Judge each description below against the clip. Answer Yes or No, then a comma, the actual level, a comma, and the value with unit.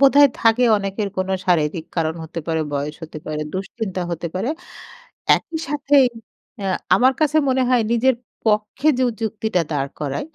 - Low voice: No, high, 200 Hz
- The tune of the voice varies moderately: No, wide, 7.7 semitones